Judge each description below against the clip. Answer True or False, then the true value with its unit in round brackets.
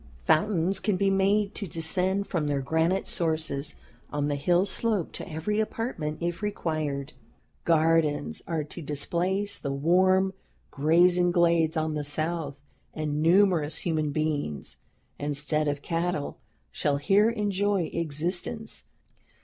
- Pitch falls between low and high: True (165 Hz)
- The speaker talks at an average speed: False (125 wpm)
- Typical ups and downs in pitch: True (3.9 semitones)